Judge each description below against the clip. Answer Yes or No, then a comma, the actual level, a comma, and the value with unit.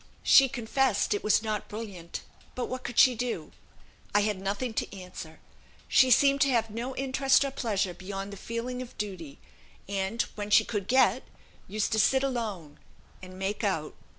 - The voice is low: No, high, 215 Hz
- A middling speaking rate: Yes, average, 175 wpm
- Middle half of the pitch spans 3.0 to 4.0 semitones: No, average, 4.5 semitones